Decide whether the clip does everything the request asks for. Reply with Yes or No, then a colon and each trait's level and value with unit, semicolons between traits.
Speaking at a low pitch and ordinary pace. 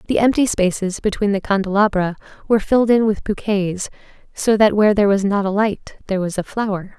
No: high, 205 Hz; average, 195 wpm